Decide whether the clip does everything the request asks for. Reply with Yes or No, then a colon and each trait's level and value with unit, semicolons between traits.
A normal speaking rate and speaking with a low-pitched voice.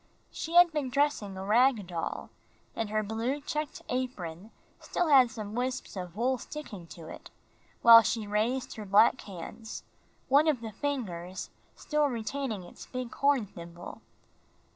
No: average, 150 wpm; high, 230 Hz